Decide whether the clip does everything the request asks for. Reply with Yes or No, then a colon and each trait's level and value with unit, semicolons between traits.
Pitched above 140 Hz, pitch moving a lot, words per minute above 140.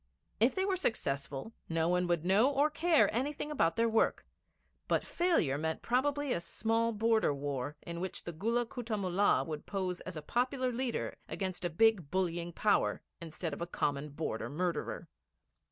Yes: high, 190 Hz; wide, 6.7 semitones; average, 170 wpm